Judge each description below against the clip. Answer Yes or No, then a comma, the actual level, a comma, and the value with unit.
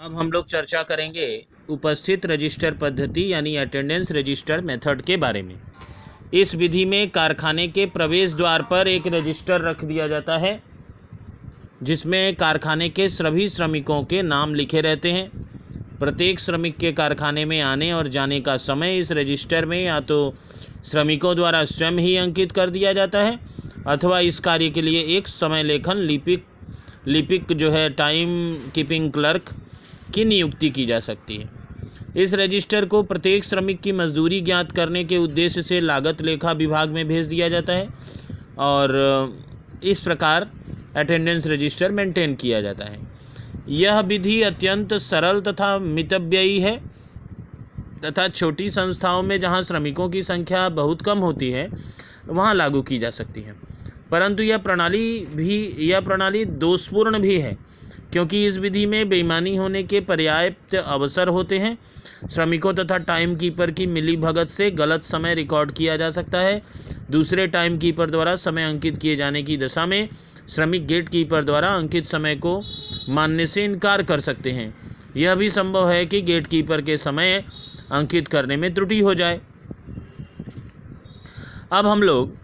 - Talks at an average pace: Yes, average, 155 wpm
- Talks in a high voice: No, medium, 165 Hz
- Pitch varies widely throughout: No, average, 3.9 semitones